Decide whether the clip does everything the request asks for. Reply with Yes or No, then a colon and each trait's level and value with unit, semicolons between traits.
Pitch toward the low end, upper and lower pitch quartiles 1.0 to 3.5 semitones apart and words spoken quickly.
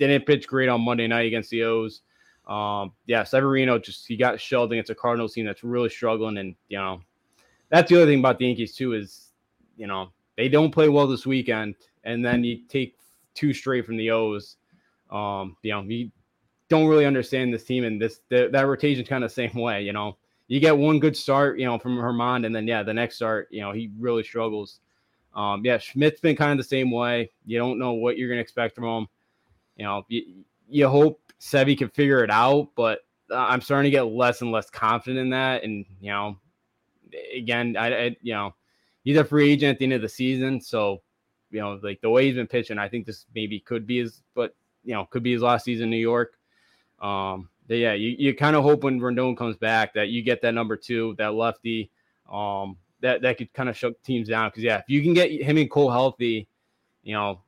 Yes: low, 120 Hz; average, 3.1 semitones; fast, 230 wpm